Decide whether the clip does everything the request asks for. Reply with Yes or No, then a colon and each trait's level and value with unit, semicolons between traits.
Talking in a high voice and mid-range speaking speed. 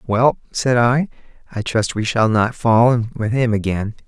No: low, 115 Hz; average, 190 wpm